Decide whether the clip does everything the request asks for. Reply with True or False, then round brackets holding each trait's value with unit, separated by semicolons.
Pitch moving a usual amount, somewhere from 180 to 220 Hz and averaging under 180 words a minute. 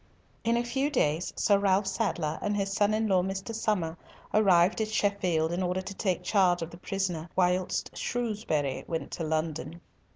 False (3.4 semitones; 190 Hz; 185 wpm)